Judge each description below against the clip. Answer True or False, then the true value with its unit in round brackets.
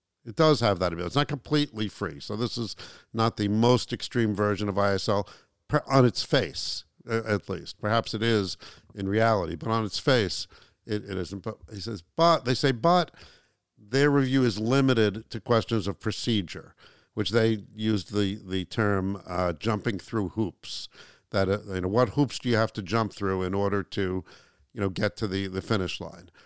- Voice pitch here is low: True (110 Hz)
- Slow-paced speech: False (195 wpm)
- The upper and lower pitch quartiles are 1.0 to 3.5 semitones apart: True (3.0 semitones)